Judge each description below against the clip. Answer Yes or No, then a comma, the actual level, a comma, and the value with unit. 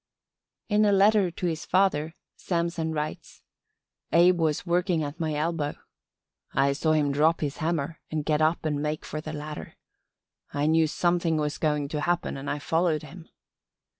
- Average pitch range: No, narrow, 2.3 semitones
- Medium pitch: Yes, medium, 160 Hz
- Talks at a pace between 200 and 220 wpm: No, average, 165 wpm